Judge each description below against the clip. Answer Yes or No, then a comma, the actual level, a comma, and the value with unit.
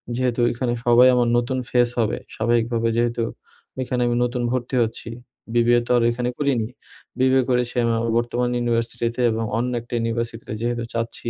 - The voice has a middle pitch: No, low, 120 Hz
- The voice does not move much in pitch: Yes, narrow, 1.0 semitones